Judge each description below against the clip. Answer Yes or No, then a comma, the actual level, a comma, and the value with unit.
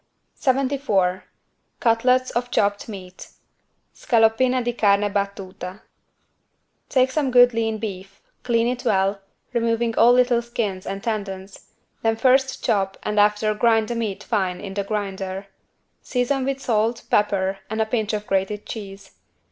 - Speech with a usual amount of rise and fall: Yes, average, 3.5 semitones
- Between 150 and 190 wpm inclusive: No, average, 140 wpm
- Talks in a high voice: Yes, high, 220 Hz